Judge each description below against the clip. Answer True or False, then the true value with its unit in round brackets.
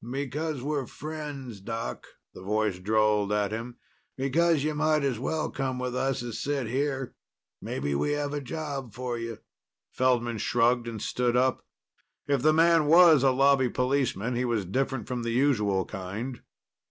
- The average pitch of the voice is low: True (125 Hz)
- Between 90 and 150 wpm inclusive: False (165 wpm)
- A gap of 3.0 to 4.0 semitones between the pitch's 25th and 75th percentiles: True (3.7 semitones)